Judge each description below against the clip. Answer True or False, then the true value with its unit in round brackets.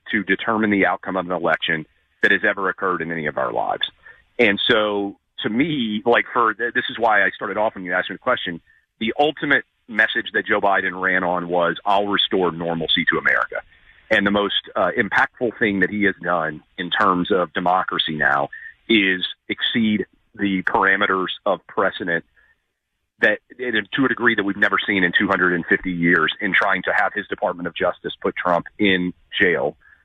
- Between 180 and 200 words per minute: True (185 wpm)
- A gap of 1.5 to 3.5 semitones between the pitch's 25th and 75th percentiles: True (3.1 semitones)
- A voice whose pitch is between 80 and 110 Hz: True (95 Hz)